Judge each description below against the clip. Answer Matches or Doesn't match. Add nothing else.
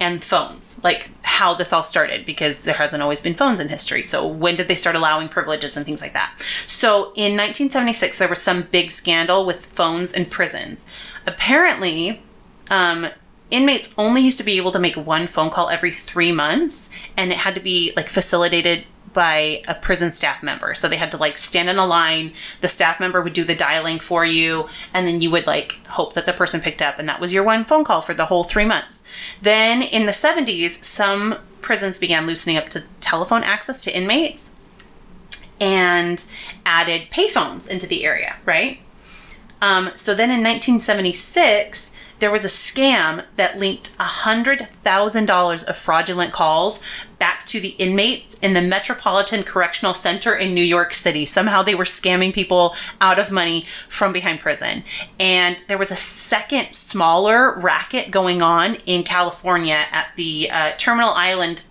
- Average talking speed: Matches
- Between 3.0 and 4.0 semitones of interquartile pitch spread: Matches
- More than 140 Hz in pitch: Matches